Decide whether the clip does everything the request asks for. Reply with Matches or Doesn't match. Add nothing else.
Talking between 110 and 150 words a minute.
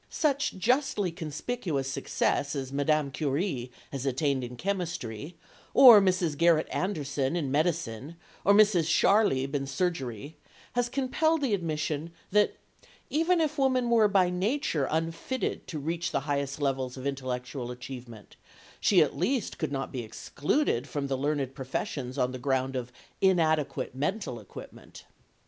Matches